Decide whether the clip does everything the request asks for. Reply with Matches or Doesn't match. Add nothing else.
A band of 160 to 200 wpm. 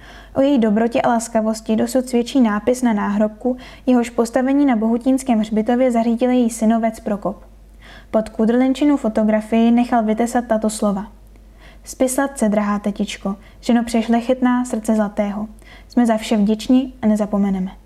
Doesn't match